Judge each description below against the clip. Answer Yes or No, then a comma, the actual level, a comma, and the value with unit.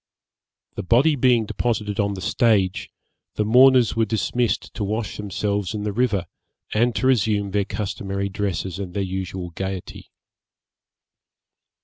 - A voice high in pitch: No, low, 105 Hz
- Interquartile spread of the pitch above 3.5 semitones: No, average, 3.0 semitones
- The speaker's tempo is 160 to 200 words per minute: No, slow, 135 wpm